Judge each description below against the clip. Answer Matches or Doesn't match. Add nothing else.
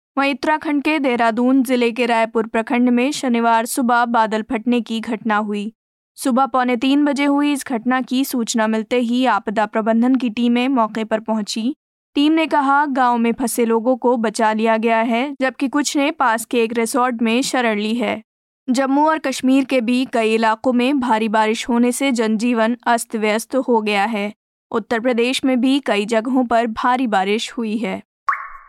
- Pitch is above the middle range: Matches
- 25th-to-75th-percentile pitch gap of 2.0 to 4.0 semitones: Matches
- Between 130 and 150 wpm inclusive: Doesn't match